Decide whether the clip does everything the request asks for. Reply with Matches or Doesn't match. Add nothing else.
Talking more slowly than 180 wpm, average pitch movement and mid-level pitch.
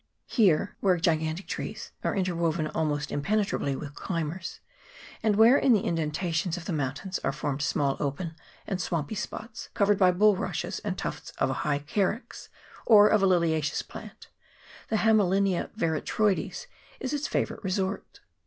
Matches